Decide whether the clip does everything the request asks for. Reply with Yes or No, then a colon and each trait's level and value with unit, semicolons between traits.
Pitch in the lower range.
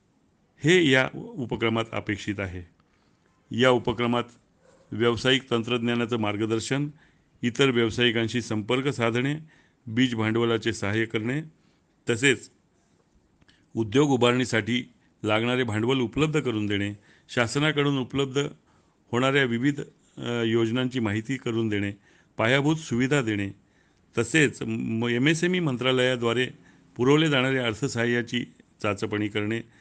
Yes: low, 120 Hz